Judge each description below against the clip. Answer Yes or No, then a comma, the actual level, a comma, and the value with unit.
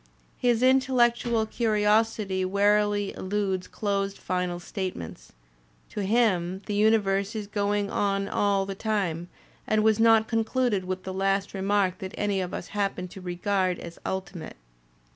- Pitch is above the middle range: Yes, high, 200 Hz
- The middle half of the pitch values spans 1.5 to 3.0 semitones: Yes, narrow, 2.4 semitones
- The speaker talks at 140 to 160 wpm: Yes, average, 150 wpm